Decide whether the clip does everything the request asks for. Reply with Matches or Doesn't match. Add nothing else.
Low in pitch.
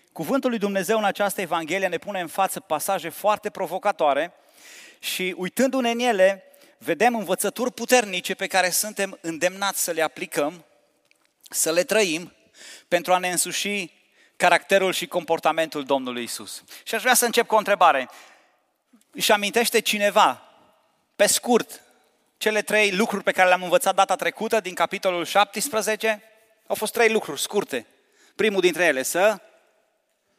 Doesn't match